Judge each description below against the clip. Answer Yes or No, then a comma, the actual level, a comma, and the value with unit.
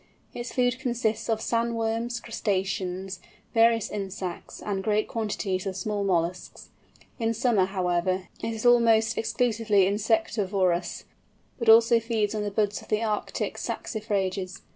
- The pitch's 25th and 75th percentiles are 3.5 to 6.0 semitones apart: No, average, 3.0 semitones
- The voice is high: Yes, high, 215 Hz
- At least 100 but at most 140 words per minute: Yes, slow, 135 wpm